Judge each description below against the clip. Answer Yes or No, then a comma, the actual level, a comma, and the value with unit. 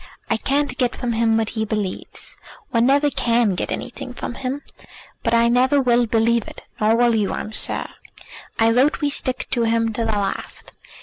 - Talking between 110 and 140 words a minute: No, average, 190 wpm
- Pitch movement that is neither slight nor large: No, narrow, 2.1 semitones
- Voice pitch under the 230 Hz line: No, high, 235 Hz